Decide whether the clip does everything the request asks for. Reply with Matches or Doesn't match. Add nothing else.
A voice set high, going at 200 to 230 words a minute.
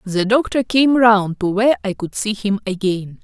Matches